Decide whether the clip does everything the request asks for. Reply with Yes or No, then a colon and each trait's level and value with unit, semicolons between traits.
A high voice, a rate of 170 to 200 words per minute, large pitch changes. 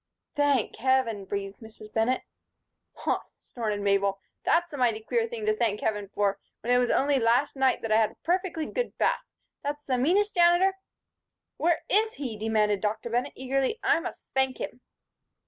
Yes: very high, 255 Hz; average, 180 wpm; wide, 6.6 semitones